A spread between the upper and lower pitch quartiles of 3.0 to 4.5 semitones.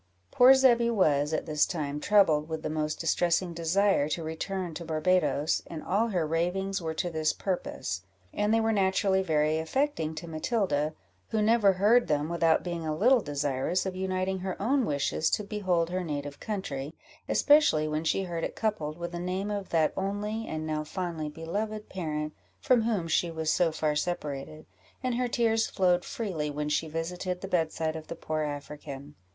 Yes: average, 4.2 semitones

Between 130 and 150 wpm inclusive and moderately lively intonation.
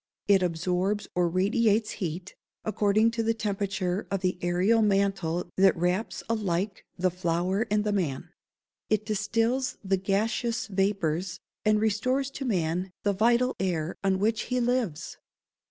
Yes: average, 140 wpm; average, 3.4 semitones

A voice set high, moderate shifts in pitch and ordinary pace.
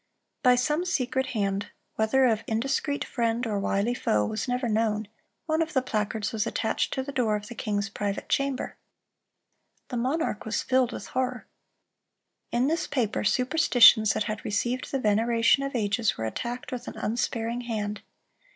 Yes: high, 235 Hz; average, 3.4 semitones; average, 160 wpm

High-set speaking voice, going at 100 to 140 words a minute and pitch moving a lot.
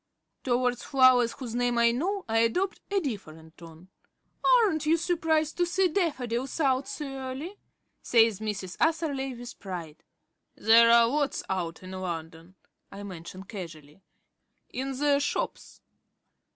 Yes: high, 245 Hz; slow, 135 wpm; wide, 7.5 semitones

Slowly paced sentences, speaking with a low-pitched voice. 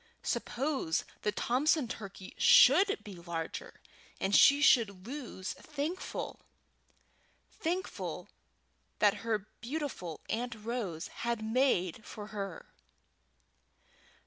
No: slow, 95 wpm; high, 225 Hz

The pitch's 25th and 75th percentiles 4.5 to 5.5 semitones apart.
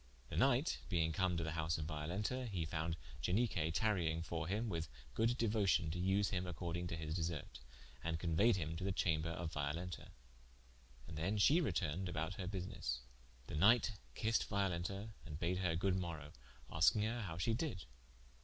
No: average, 3.8 semitones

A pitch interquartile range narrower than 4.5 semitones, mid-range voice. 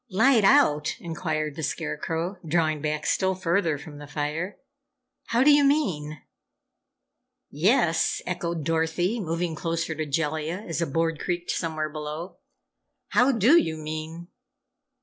Yes: average, 3.1 semitones; medium, 165 Hz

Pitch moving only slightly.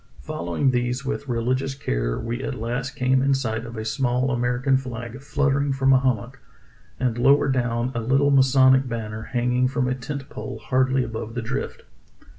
Yes: narrow, 2.1 semitones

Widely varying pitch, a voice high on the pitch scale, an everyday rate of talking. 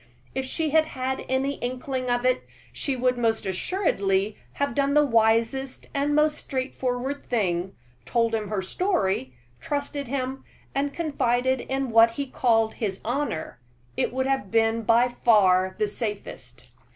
No: average, 3.8 semitones; high, 245 Hz; average, 150 wpm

